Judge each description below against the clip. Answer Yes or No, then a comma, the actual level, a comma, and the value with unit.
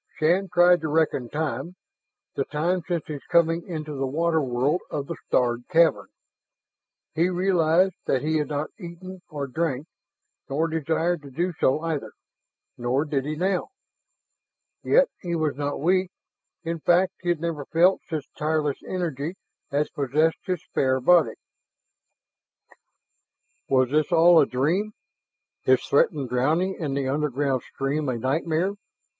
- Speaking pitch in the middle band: Yes, medium, 155 Hz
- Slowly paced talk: No, average, 145 wpm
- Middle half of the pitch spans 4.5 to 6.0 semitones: No, average, 3.7 semitones